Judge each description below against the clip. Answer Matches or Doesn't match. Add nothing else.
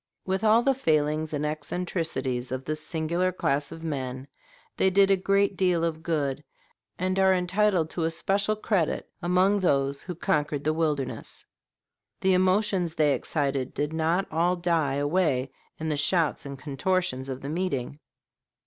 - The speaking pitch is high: Doesn't match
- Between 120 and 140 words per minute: Doesn't match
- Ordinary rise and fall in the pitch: Matches